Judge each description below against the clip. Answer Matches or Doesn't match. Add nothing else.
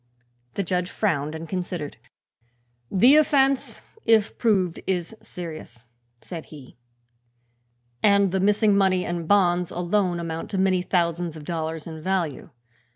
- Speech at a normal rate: Doesn't match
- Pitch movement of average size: Matches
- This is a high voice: Doesn't match